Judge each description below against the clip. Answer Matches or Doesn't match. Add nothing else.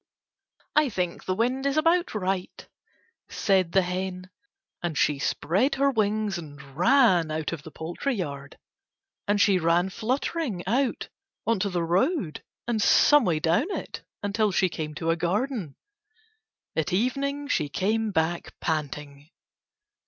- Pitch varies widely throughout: Matches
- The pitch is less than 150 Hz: Doesn't match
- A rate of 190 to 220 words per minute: Doesn't match